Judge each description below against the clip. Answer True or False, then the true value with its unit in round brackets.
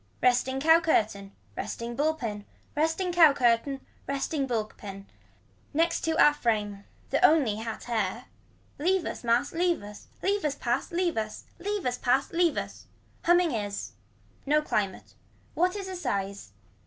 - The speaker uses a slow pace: False (155 wpm)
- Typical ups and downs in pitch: False (7.0 semitones)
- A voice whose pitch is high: True (270 Hz)